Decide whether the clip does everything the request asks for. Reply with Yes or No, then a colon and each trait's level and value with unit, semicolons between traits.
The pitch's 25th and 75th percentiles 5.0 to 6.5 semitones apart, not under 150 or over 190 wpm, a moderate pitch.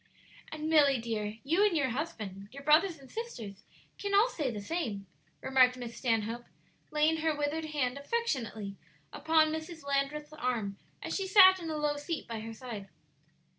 No: wide, 5.6 semitones; average, 170 wpm; very high, 285 Hz